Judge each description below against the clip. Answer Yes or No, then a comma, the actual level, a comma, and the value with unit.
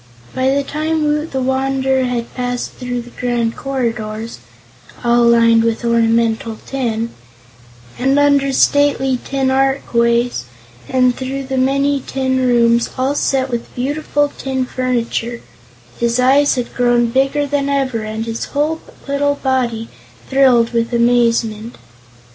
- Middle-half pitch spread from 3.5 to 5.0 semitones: No, narrow, 2.5 semitones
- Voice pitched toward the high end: Yes, very high, 255 Hz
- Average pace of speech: No, slow, 130 wpm